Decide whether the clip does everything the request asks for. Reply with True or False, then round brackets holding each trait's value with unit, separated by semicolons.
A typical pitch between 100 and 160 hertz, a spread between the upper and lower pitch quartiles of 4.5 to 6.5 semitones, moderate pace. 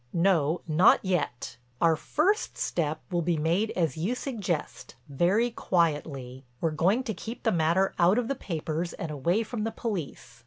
False (175 Hz; 5.5 semitones; 165 wpm)